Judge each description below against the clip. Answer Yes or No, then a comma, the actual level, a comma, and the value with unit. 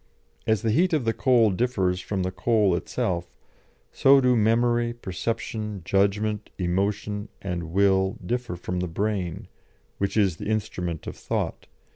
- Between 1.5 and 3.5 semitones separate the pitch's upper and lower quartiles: No, average, 3.9 semitones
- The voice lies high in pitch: No, low, 105 Hz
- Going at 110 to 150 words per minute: Yes, average, 145 wpm